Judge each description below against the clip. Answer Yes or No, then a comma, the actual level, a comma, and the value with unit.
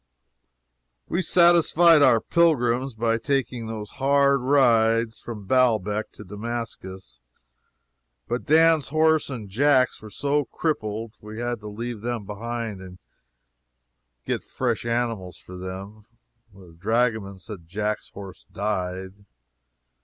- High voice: No, low, 115 Hz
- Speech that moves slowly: Yes, slow, 115 wpm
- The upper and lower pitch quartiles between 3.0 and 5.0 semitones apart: Yes, average, 4.2 semitones